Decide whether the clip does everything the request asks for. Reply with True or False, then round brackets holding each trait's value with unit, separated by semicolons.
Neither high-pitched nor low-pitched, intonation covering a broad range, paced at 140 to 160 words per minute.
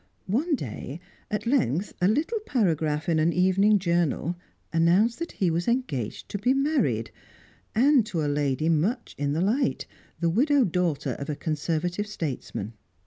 True (180 Hz; 7.1 semitones; 155 wpm)